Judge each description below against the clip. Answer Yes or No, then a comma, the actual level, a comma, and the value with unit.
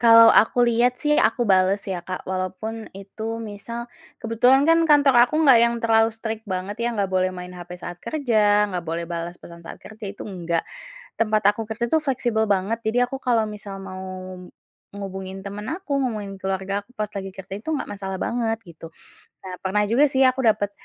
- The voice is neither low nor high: No, high, 210 Hz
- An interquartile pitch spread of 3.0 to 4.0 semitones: Yes, average, 3.7 semitones